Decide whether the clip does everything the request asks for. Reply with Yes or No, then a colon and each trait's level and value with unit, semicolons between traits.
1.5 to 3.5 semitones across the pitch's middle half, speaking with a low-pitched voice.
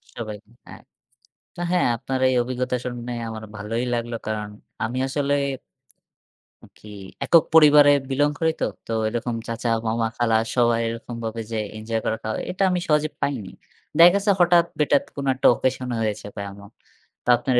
No: average, 4.3 semitones; low, 120 Hz